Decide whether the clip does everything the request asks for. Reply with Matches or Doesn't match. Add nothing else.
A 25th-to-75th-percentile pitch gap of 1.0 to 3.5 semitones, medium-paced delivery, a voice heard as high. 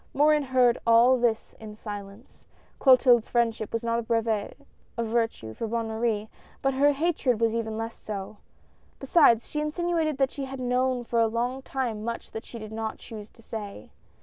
Matches